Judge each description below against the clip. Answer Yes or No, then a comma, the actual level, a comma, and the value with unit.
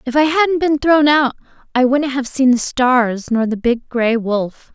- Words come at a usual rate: No, fast, 215 wpm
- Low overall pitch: No, very high, 260 Hz